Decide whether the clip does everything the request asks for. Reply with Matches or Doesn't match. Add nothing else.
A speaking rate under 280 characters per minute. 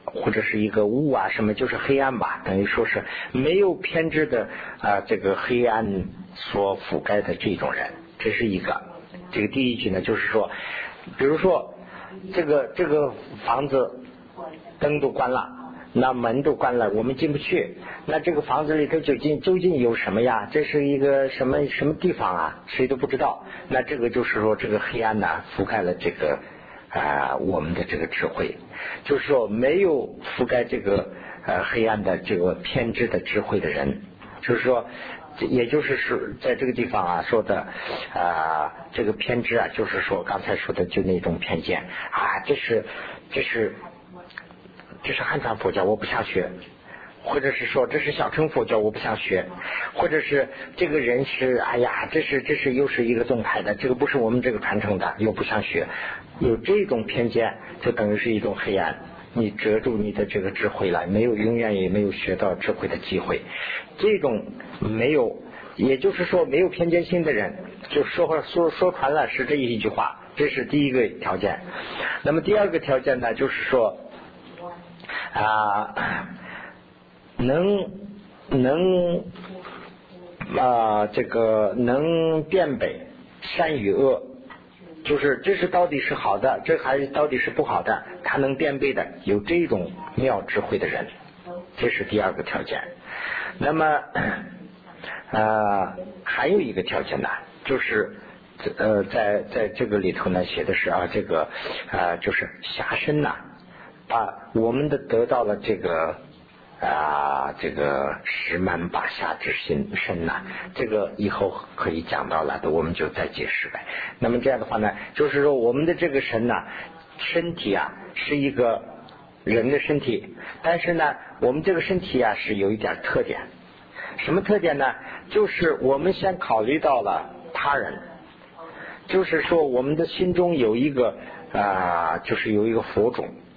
Matches